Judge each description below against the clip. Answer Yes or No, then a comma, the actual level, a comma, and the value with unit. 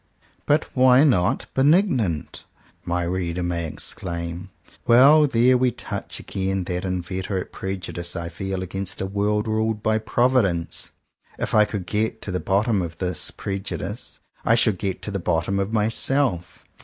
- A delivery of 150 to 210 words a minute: Yes, average, 155 wpm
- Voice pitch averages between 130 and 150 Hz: No, low, 100 Hz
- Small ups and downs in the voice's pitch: No, average, 4.0 semitones